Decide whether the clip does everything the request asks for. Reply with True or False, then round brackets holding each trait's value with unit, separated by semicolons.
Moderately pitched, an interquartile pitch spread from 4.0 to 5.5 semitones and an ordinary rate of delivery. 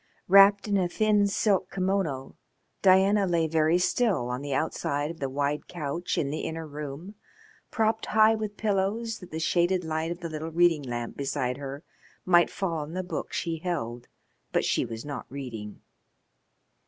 True (165 Hz; 5.1 semitones; 170 wpm)